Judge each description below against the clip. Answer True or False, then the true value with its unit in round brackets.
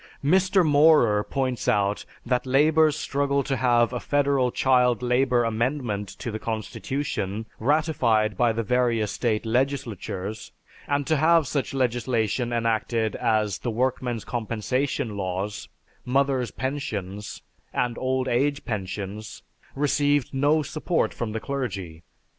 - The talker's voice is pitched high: False (125 Hz)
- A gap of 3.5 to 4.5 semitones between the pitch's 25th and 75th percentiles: True (4.2 semitones)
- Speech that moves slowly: True (125 wpm)